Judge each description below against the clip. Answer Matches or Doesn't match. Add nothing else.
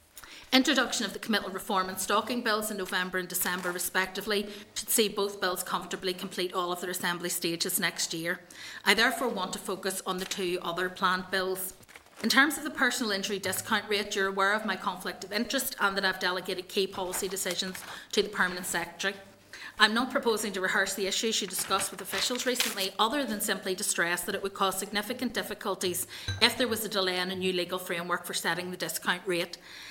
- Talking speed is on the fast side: Matches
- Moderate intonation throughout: Doesn't match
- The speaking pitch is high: Matches